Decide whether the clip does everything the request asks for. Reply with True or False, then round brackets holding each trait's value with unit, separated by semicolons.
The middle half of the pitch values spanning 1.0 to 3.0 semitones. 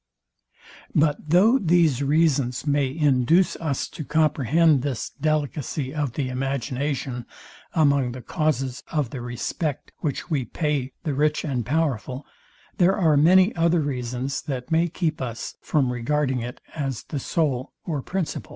False (3.6 semitones)